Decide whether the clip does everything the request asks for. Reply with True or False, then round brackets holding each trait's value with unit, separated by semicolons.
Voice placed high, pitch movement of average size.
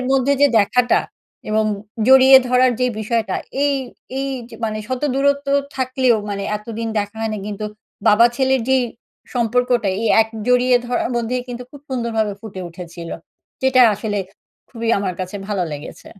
True (235 Hz; 3.3 semitones)